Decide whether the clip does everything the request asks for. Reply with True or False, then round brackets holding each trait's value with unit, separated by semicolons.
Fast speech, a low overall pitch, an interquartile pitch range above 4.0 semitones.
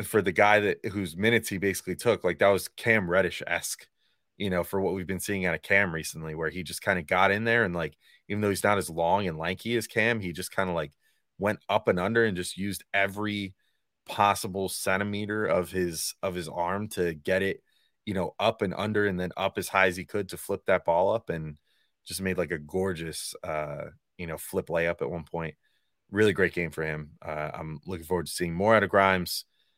False (235 wpm; 95 Hz; 2.9 semitones)